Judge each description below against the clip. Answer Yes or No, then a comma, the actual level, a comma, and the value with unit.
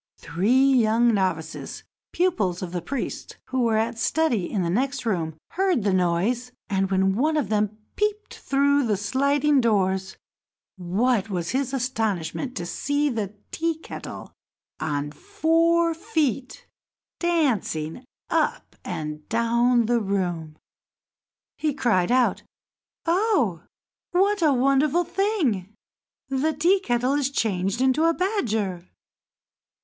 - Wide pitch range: Yes, wide, 7.5 semitones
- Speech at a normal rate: No, slow, 125 wpm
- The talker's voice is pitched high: Yes, high, 240 Hz